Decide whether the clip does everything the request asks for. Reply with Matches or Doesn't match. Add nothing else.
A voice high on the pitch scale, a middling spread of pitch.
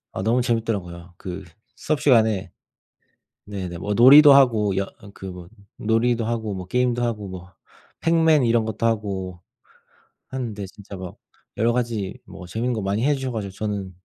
Doesn't match